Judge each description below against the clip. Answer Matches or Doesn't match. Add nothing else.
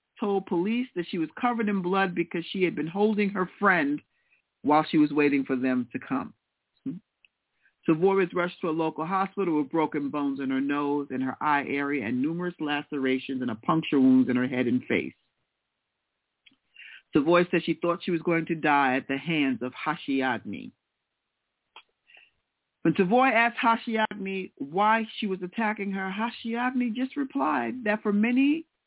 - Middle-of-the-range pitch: Matches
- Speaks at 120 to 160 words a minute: Doesn't match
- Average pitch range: Doesn't match